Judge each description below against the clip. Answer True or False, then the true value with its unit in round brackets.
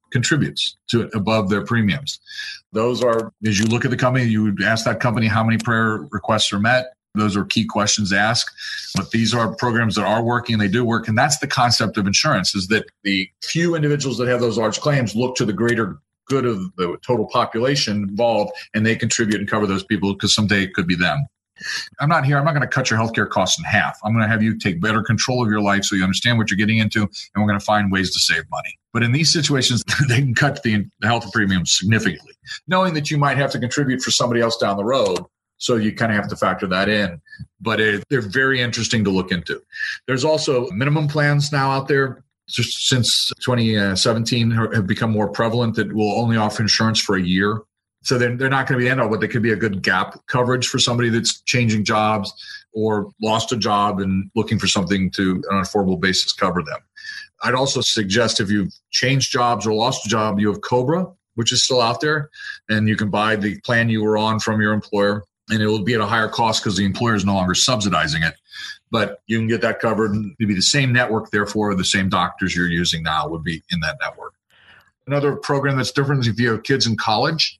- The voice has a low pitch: True (115 Hz)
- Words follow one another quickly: True (235 wpm)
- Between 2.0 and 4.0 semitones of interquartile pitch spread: True (3.1 semitones)